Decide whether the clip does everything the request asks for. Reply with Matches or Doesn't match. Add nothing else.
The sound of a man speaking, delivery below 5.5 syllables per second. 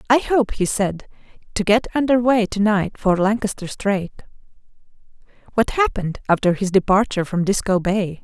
Doesn't match